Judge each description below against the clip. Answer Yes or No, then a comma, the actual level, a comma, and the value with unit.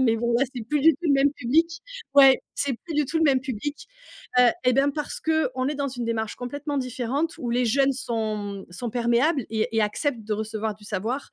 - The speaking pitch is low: No, very high, 255 Hz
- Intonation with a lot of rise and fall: No, average, 4.1 semitones